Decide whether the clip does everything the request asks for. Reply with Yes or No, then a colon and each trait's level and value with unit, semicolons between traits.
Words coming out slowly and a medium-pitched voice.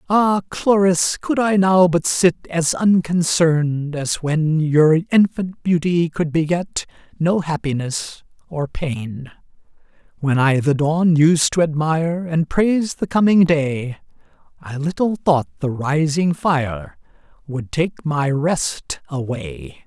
Yes: slow, 130 wpm; medium, 160 Hz